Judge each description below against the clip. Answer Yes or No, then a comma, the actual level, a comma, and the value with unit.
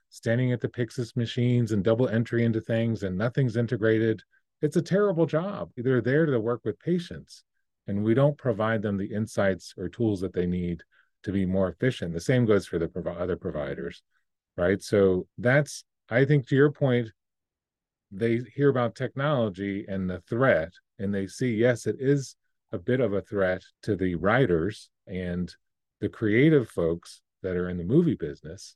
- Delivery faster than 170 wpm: Yes, average, 180 wpm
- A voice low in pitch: Yes, low, 115 Hz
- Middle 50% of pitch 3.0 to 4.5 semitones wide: No, average, 4.9 semitones